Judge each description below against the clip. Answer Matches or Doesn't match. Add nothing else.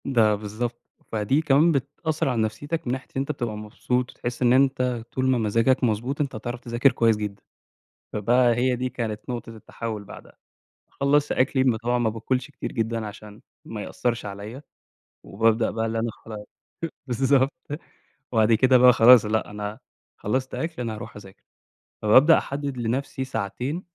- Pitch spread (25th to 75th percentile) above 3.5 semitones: Doesn't match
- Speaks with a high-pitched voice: Doesn't match